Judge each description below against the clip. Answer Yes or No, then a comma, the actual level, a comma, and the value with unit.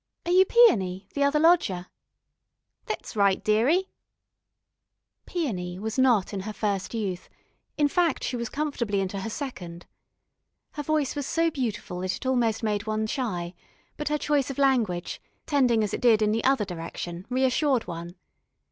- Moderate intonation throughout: No, wide, 6.5 semitones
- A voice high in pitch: Yes, high, 225 Hz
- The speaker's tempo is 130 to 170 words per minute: Yes, average, 160 wpm